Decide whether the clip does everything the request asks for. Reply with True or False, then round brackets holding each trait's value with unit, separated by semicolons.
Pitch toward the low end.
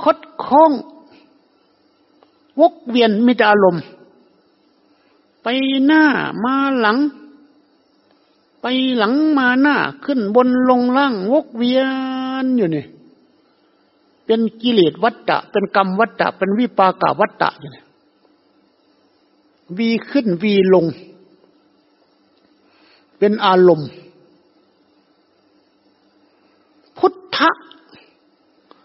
False (255 Hz)